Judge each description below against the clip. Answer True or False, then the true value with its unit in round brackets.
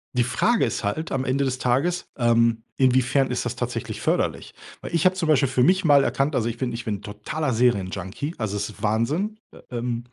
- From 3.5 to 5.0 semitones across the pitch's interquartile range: True (3.9 semitones)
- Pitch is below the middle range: True (125 Hz)